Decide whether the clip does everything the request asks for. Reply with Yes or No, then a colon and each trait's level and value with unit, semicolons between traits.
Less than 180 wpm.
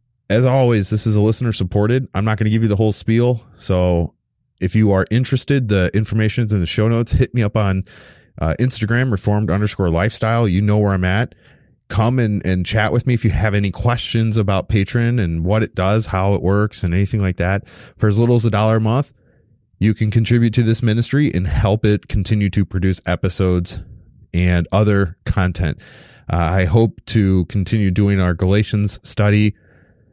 No: average, 195 wpm